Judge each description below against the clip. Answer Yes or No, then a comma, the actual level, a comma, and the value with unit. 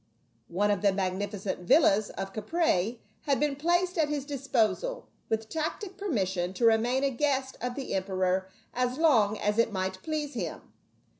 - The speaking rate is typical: Yes, average, 160 wpm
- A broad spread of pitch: Yes, wide, 7.0 semitones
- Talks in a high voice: Yes, high, 230 Hz